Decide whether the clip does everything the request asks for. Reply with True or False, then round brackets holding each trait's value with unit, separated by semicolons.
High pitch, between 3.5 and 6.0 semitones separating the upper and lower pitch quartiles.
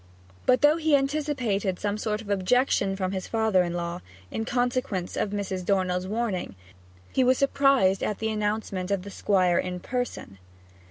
True (205 Hz; 4.9 semitones)